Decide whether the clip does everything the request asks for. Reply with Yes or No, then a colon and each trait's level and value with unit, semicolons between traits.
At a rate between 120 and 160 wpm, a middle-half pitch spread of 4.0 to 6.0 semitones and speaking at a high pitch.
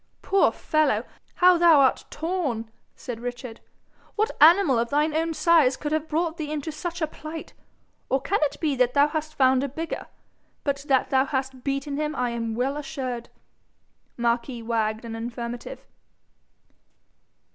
Yes: average, 155 wpm; average, 4.3 semitones; very high, 280 Hz